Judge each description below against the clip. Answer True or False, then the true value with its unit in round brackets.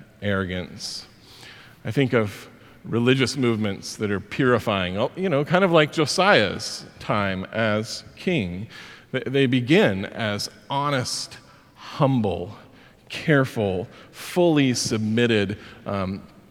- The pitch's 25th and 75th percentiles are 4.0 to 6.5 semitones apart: True (4.7 semitones)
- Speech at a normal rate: False (100 wpm)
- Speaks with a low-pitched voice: True (115 Hz)